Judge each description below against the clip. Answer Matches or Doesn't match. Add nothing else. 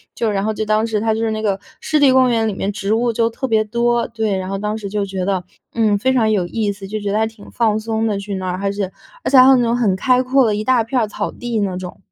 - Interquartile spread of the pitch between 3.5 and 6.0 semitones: Doesn't match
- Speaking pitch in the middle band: Doesn't match